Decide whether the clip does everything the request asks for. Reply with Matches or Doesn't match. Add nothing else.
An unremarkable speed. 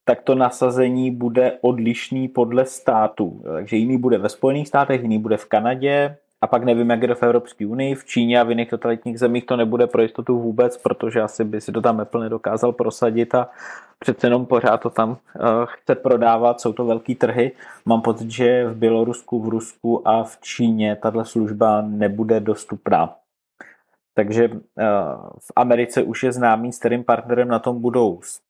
Doesn't match